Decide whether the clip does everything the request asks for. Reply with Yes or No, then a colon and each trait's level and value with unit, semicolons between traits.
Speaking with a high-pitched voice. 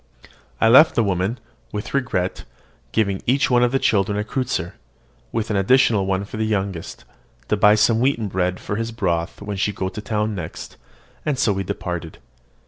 No: low, 105 Hz